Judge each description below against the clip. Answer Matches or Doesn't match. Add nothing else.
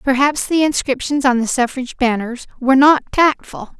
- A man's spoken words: Doesn't match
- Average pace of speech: Matches